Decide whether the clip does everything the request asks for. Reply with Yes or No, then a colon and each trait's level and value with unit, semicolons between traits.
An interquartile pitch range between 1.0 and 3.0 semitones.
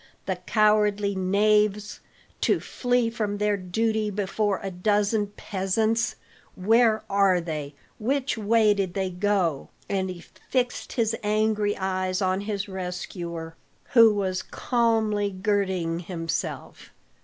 Yes: narrow, 2.5 semitones